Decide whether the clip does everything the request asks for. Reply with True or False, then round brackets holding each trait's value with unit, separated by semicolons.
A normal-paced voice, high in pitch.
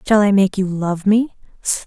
True (195 wpm; 200 Hz)